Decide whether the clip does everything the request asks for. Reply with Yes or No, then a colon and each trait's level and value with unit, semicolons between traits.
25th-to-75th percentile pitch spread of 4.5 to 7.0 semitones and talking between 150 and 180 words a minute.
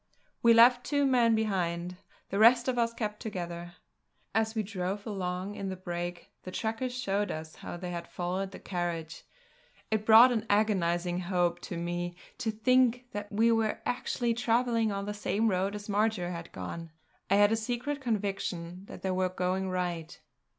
No: average, 4.1 semitones; average, 175 wpm